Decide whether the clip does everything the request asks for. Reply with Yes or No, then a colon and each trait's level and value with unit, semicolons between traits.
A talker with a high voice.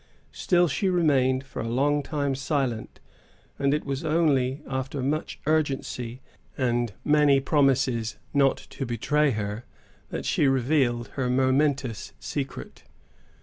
No: low, 135 Hz